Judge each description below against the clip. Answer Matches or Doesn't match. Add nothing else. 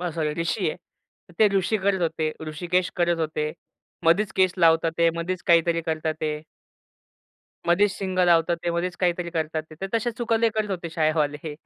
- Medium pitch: Matches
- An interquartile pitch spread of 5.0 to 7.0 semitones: Doesn't match